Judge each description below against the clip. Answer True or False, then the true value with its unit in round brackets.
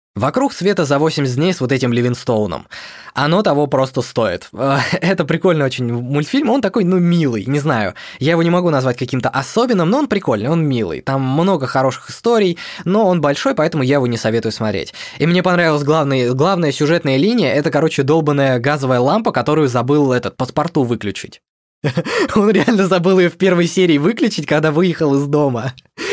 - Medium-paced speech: False (175 wpm)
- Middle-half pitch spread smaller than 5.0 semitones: False (5.4 semitones)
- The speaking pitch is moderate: True (150 Hz)